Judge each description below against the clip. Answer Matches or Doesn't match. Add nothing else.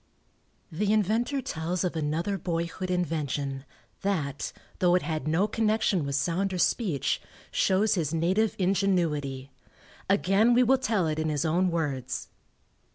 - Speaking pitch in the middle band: Matches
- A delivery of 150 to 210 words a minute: Doesn't match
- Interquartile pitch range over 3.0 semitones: Matches